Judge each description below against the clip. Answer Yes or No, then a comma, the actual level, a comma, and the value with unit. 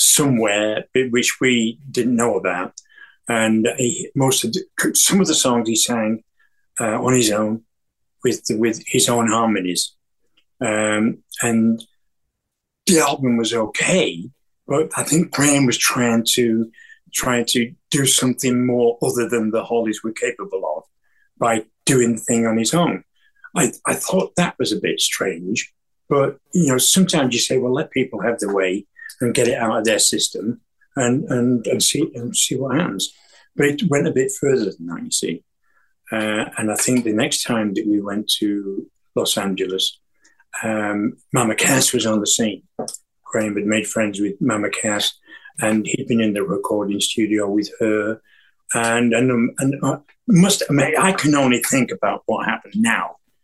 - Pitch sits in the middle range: No, low, 120 Hz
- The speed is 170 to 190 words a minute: Yes, average, 175 wpm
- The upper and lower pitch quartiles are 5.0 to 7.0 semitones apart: No, average, 3.4 semitones